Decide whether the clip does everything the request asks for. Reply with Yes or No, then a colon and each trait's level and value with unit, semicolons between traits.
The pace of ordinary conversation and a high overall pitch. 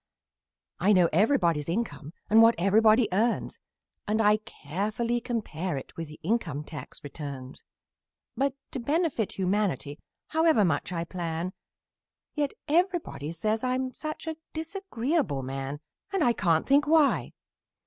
No: slow, 130 wpm; high, 215 Hz